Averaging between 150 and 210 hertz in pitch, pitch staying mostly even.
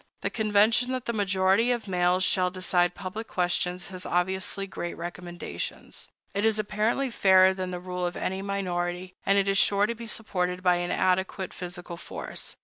Yes: high, 190 Hz; narrow, 2.3 semitones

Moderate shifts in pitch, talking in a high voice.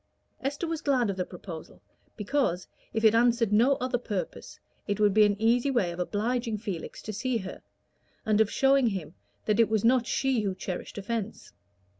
Yes: average, 3.5 semitones; high, 220 Hz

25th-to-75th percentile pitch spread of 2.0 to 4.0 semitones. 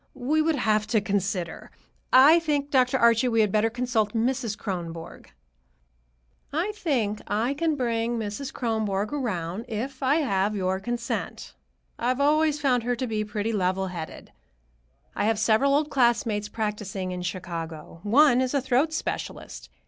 No: average, 4.5 semitones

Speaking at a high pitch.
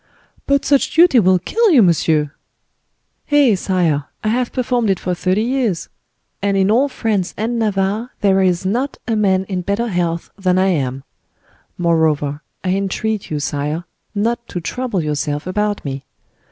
Yes: high, 195 Hz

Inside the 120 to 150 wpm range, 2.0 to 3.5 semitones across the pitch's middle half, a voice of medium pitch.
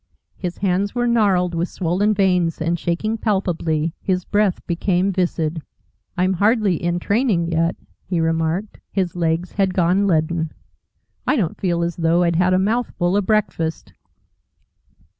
Yes: average, 145 wpm; average, 2.9 semitones; medium, 180 Hz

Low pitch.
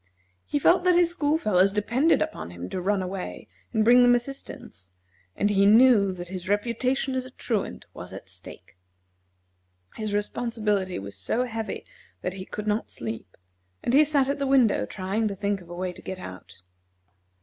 No: high, 210 Hz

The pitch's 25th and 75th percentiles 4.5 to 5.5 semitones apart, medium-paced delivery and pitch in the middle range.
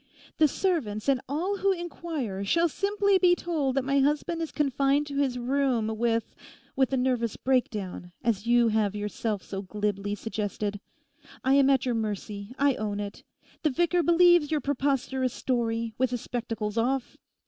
No: average, 5.1 semitones; average, 160 wpm; very high, 255 Hz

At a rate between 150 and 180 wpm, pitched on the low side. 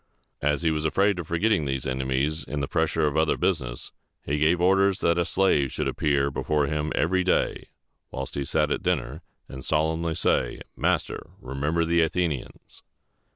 Yes: average, 170 wpm; very low, 80 Hz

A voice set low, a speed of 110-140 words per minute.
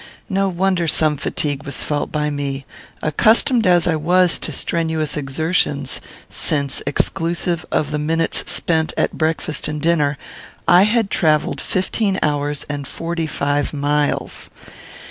No: medium, 155 Hz; slow, 135 wpm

